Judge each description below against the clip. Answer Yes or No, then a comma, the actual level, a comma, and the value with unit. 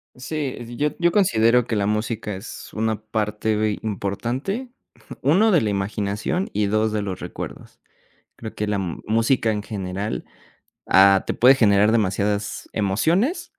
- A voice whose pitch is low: Yes, low, 110 Hz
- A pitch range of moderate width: Yes, average, 3.7 semitones